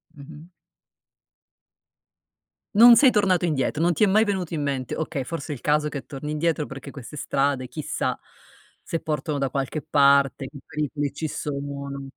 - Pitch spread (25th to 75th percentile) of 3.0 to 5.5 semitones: No, narrow, 2.6 semitones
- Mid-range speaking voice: Yes, medium, 150 Hz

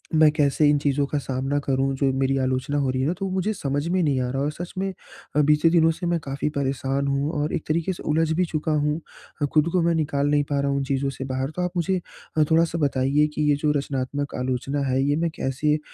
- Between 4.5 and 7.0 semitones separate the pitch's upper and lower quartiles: No, average, 2.7 semitones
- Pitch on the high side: No, medium, 145 Hz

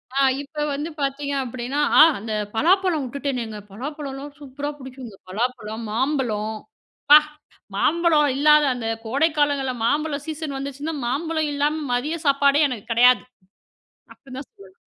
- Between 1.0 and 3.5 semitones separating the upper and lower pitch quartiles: Yes, average, 3.2 semitones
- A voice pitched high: Yes, very high, 280 Hz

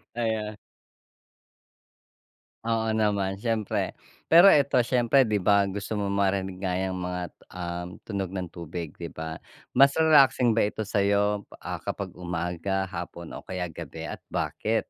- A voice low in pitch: Yes, low, 100 Hz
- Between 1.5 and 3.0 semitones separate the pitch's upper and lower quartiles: No, average, 3.5 semitones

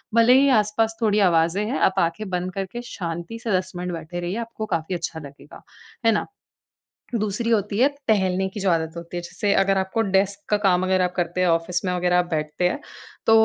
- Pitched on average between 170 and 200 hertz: Yes, medium, 185 Hz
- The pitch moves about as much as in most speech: Yes, average, 3.2 semitones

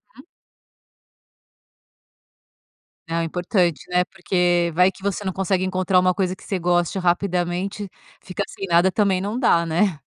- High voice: No, medium, 180 Hz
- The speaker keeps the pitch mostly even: Yes, narrow, 1.7 semitones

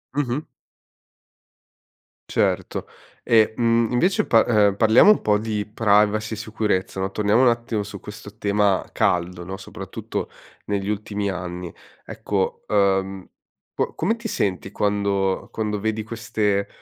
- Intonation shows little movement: Yes, narrow, 2.1 semitones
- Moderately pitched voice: No, low, 105 Hz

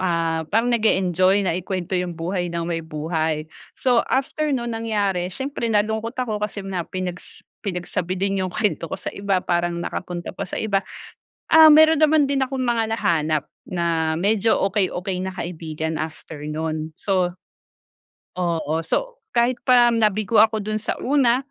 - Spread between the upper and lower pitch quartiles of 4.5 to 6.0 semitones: Yes, average, 4.8 semitones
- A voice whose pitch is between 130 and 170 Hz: No, high, 190 Hz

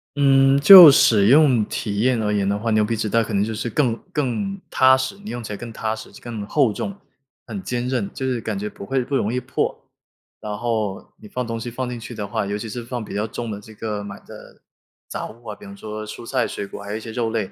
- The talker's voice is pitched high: No, low, 115 Hz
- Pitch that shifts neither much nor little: Yes, average, 3.4 semitones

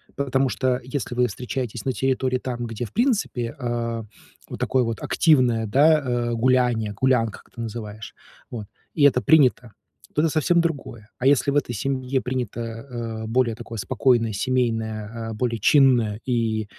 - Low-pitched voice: Yes, low, 120 Hz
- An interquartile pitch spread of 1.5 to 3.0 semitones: Yes, narrow, 2.6 semitones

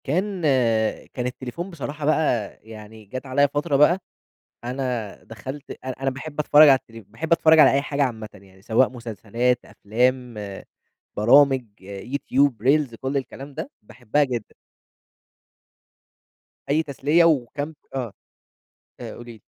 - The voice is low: Yes, low, 130 Hz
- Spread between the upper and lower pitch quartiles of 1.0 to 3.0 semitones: No, average, 3.9 semitones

